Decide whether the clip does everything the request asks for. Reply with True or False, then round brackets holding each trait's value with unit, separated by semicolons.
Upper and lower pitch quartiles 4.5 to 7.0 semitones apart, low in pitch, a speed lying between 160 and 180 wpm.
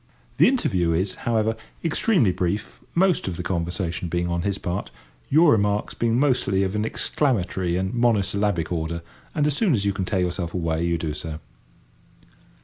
True (4.9 semitones; 95 Hz; 175 wpm)